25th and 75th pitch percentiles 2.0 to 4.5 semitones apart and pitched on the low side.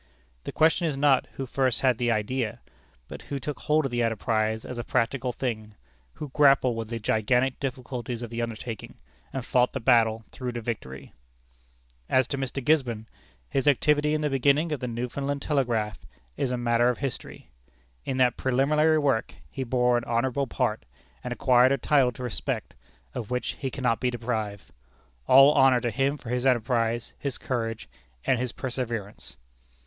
Yes: narrow, 2.6 semitones; low, 125 Hz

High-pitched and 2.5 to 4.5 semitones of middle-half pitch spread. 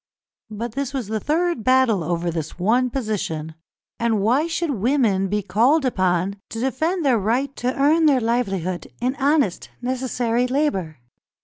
No: high, 240 Hz; wide, 5.5 semitones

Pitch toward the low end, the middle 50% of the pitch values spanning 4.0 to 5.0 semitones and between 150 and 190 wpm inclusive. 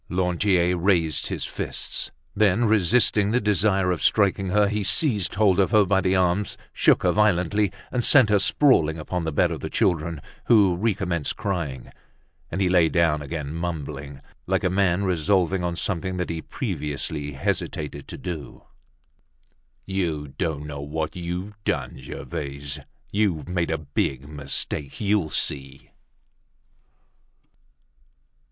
No: very low, 90 Hz; average, 4.5 semitones; average, 140 wpm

